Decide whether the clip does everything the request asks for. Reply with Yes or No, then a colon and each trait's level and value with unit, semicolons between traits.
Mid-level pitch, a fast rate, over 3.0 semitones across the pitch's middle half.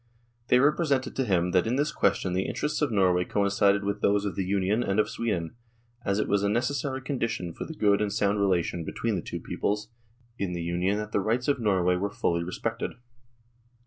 No: low, 100 Hz; fast, 210 wpm; average, 3.8 semitones